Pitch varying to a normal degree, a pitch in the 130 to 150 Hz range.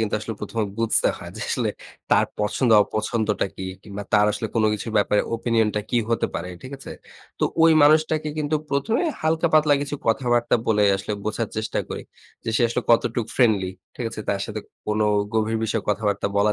No: average, 3.1 semitones; low, 115 Hz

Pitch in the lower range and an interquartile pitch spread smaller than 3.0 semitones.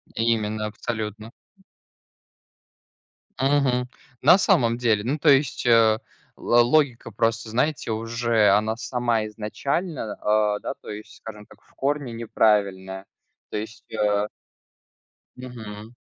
Yes: low, 115 Hz; narrow, 2.6 semitones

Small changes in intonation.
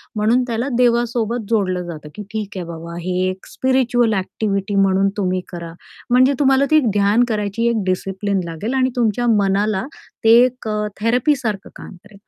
No: average, 3.8 semitones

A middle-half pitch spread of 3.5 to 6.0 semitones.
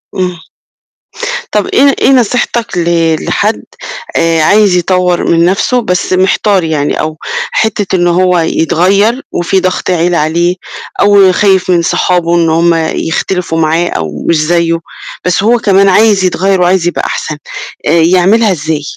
No: average, 2.7 semitones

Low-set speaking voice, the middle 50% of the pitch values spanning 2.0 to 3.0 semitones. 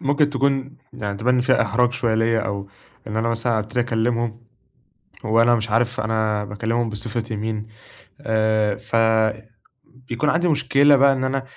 Yes: low, 115 Hz; narrow, 2.6 semitones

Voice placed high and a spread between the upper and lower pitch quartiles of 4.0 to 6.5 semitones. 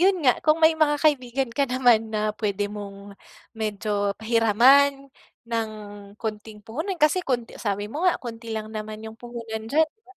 Yes: high, 230 Hz; average, 4.7 semitones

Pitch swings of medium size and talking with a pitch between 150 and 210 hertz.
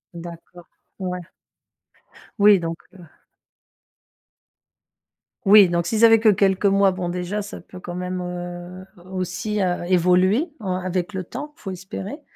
No: narrow, 2.1 semitones; medium, 185 Hz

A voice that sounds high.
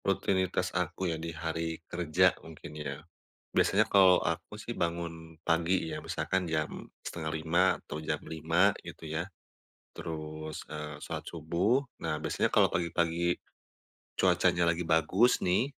No: very low, 85 Hz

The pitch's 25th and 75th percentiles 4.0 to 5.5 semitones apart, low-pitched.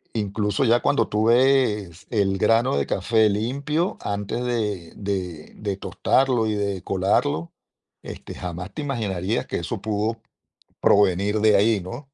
No: average, 3.2 semitones; low, 105 Hz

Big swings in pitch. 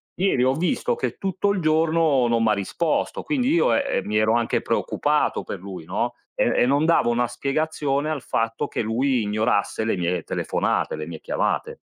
Yes: wide, 6.8 semitones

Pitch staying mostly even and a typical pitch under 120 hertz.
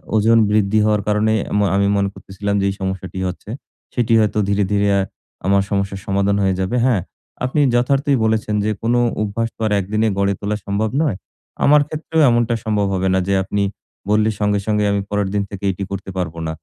Yes: narrow, 1.9 semitones; low, 105 Hz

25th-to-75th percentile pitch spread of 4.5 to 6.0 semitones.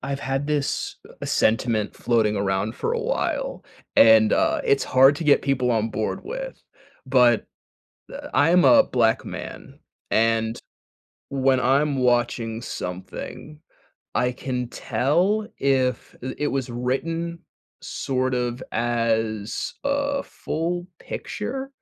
Yes: average, 4.8 semitones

